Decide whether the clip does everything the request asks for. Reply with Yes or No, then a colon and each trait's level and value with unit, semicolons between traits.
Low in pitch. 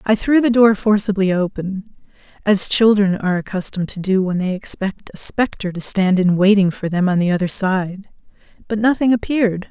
No: high, 200 Hz